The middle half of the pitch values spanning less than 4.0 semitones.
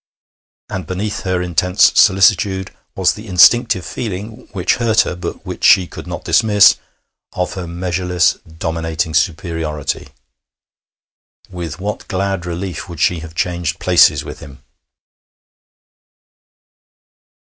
Yes: average, 2.7 semitones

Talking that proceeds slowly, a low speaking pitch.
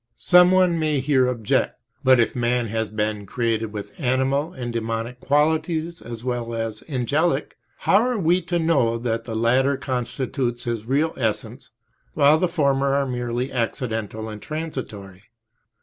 No: average, 150 wpm; low, 125 Hz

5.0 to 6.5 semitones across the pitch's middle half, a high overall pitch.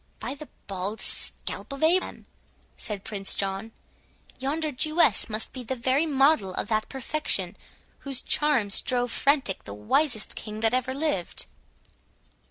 Yes: wide, 5.4 semitones; very high, 255 Hz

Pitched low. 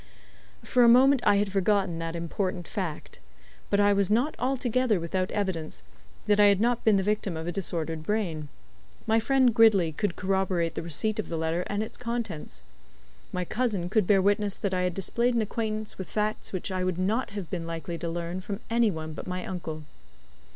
No: high, 195 Hz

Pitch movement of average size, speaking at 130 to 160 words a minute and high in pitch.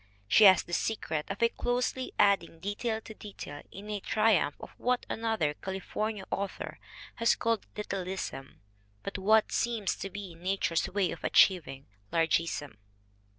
Yes: average, 4.5 semitones; average, 140 wpm; high, 195 Hz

